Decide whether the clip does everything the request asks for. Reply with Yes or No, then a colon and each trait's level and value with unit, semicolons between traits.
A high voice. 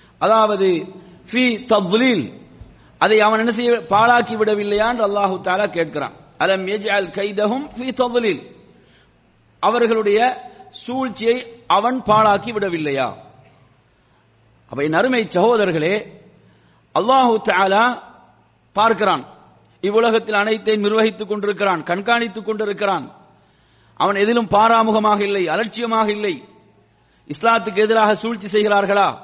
Yes: high, 215 Hz